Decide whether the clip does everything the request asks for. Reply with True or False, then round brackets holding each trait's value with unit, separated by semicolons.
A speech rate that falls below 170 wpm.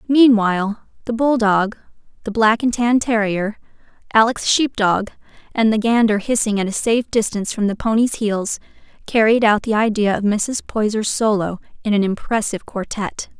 True (160 wpm)